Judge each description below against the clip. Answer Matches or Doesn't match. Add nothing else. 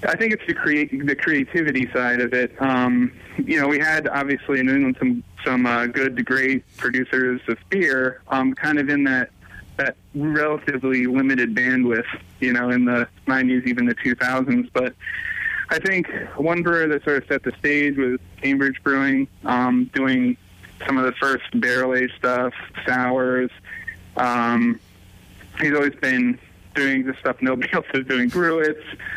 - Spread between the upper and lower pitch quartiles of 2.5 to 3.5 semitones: Matches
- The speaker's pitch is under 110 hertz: Doesn't match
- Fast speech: Doesn't match